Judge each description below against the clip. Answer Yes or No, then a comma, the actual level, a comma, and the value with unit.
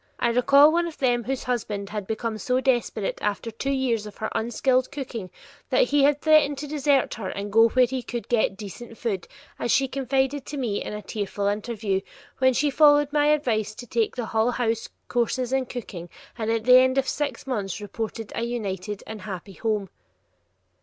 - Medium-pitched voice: No, high, 240 Hz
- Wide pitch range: No, average, 3.8 semitones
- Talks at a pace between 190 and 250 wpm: Yes, average, 195 wpm